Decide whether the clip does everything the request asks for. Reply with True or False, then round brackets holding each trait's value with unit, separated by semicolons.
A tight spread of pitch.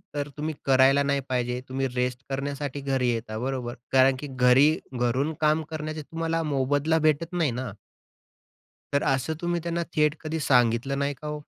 False (3.1 semitones)